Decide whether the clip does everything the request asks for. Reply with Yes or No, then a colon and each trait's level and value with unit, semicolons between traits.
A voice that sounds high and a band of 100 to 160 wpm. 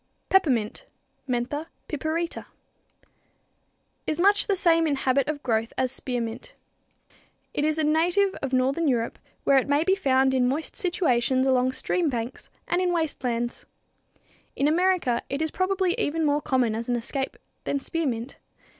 Yes: very high, 285 Hz; average, 155 wpm